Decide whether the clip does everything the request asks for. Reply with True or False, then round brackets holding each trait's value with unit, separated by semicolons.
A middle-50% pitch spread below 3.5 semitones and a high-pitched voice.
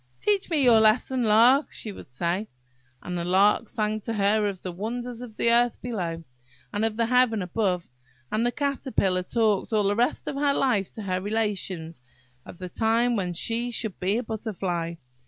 False (4.1 semitones; 215 Hz)